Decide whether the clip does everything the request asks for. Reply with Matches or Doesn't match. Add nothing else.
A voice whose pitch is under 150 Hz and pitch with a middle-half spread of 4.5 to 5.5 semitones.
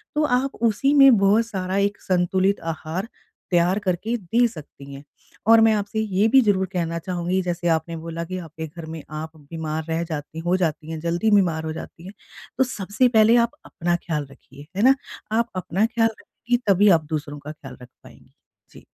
Doesn't match